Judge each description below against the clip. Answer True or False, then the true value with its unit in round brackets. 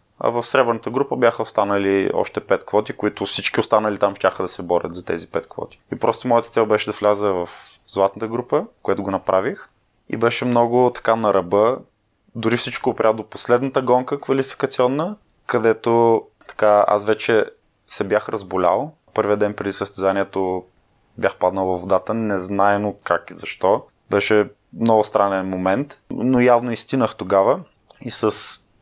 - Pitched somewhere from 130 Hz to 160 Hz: False (110 Hz)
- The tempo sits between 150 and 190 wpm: True (160 wpm)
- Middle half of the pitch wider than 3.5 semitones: False (3.1 semitones)